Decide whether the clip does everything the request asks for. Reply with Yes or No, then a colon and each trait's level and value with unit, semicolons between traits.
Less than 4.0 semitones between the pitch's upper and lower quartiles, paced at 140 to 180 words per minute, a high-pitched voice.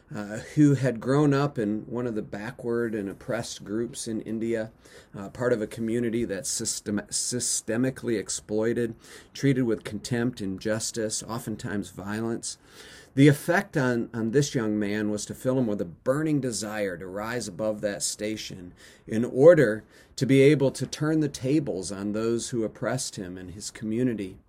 No: average, 3.4 semitones; average, 165 wpm; low, 115 Hz